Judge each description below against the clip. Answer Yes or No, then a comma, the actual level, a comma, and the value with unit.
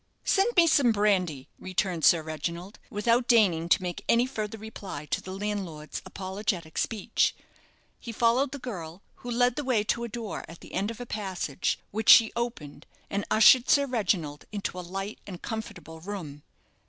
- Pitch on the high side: Yes, high, 205 Hz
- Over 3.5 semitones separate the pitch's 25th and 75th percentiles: Yes, average, 5.1 semitones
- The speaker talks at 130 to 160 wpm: No, average, 175 wpm